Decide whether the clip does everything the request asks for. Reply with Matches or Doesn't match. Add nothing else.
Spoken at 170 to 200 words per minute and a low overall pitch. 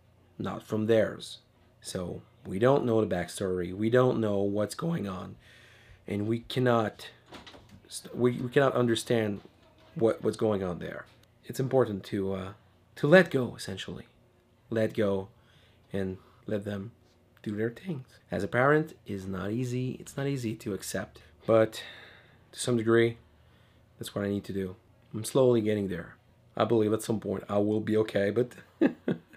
Doesn't match